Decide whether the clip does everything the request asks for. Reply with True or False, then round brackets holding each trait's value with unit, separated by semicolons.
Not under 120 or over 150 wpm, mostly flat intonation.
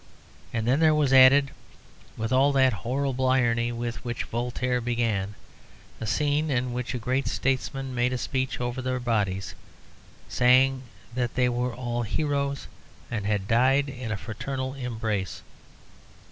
True (145 wpm; 2.1 semitones)